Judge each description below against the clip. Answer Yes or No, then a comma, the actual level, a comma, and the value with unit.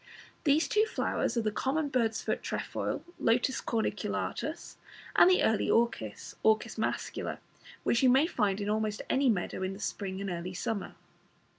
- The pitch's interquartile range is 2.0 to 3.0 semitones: No, average, 4.4 semitones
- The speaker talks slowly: No, average, 165 wpm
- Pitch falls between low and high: No, high, 220 Hz